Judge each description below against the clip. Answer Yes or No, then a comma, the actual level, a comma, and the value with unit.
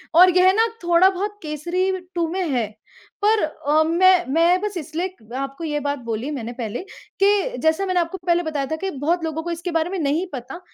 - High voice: Yes, very high, 340 Hz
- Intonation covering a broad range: No, average, 3.7 semitones